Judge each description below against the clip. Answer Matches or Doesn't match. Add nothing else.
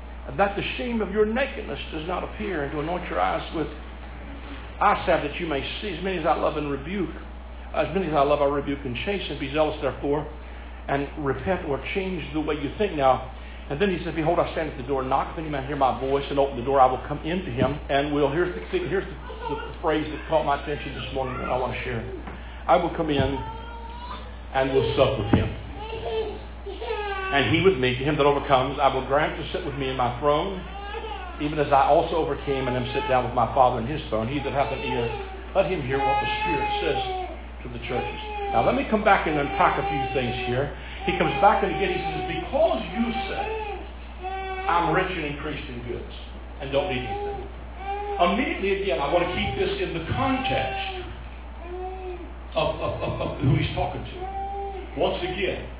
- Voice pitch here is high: Doesn't match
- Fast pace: Matches